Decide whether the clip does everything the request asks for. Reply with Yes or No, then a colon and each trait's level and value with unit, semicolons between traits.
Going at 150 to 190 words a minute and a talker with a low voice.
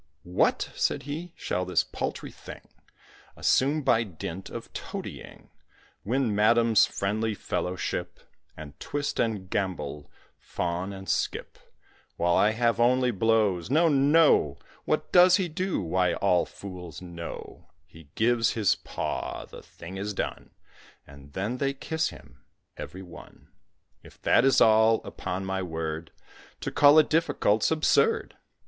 No: average, 140 wpm; low, 105 Hz